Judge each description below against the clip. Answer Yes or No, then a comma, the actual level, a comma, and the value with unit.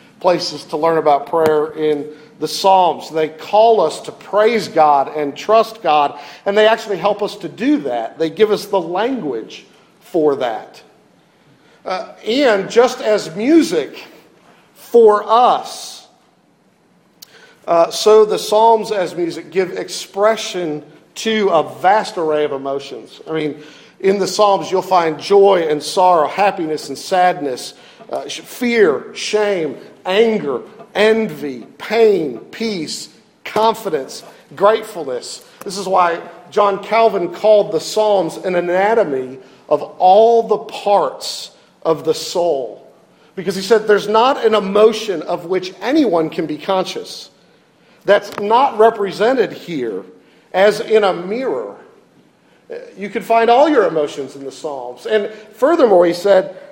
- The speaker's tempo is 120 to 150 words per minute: Yes, slow, 135 wpm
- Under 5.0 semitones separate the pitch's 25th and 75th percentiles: No, average, 5.3 semitones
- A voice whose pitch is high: Yes, high, 200 Hz